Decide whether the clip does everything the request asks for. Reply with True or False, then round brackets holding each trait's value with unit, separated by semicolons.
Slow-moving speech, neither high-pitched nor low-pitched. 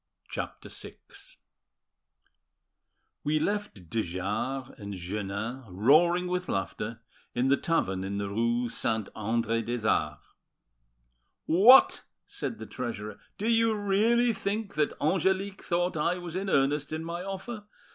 True (130 wpm; 150 Hz)